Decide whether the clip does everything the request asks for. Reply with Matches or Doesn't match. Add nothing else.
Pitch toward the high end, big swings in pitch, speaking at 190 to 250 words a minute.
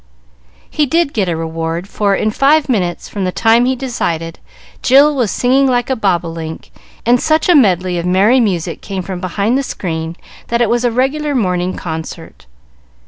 Doesn't match